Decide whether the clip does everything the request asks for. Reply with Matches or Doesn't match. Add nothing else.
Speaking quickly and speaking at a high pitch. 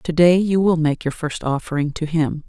Doesn't match